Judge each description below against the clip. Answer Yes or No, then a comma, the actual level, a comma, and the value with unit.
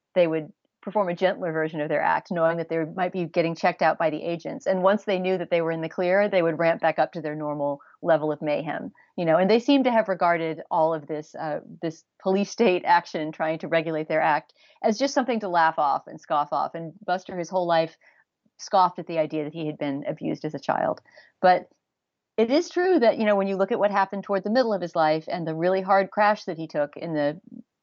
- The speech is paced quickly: Yes, fast, 250 wpm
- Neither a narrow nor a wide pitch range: Yes, average, 3.5 semitones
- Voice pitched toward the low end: No, medium, 175 Hz